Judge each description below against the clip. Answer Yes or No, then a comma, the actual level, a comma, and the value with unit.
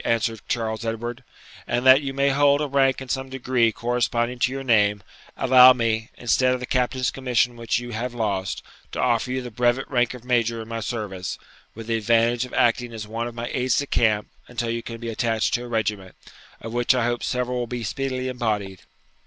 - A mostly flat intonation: Yes, narrow, 2.0 semitones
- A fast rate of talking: Yes, fast, 210 wpm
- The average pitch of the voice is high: No, low, 120 Hz